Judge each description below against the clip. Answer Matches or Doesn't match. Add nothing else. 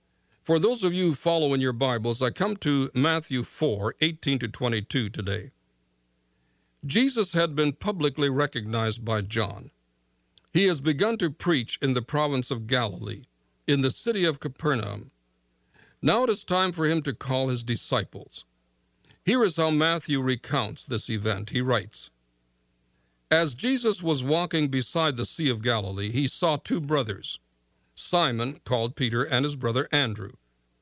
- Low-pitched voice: Matches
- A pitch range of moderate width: Doesn't match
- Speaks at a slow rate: Doesn't match